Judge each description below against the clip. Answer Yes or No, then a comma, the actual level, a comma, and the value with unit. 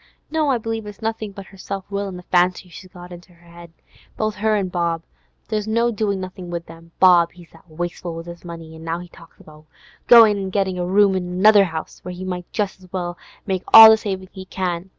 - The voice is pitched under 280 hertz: Yes, medium, 185 Hz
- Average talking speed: No, fast, 235 wpm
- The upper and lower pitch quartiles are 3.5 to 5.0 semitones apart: No, average, 2.9 semitones